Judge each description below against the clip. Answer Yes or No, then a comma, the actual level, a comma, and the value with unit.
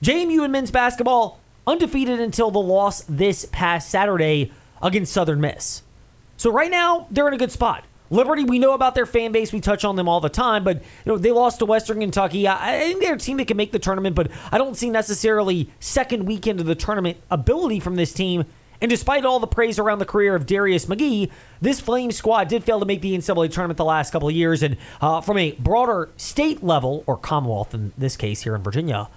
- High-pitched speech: Yes, high, 200 Hz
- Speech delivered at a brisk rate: Yes, fast, 225 wpm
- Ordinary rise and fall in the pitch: No, wide, 6.3 semitones